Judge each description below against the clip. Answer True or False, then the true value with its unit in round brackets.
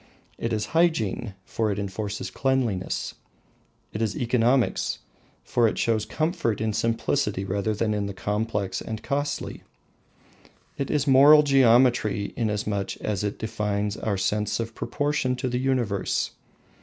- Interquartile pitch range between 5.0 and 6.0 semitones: False (3.9 semitones)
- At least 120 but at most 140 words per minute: True (135 wpm)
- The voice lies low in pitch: True (110 Hz)